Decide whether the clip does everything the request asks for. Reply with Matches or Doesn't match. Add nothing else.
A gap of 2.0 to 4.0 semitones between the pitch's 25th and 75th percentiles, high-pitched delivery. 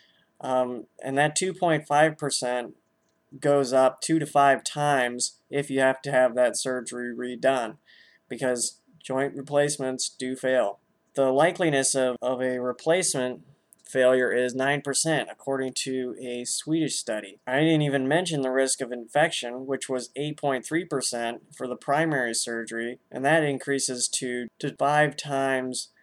Doesn't match